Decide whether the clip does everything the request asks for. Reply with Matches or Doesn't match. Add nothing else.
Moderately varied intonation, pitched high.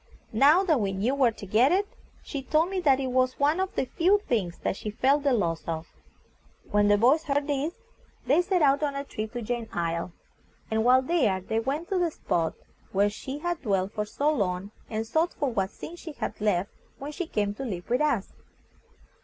Doesn't match